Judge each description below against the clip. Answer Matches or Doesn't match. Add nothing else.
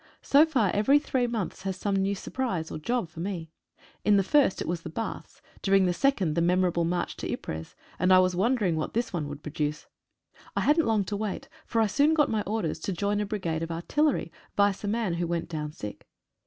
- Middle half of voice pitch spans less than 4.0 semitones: Doesn't match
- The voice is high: Matches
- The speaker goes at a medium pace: Doesn't match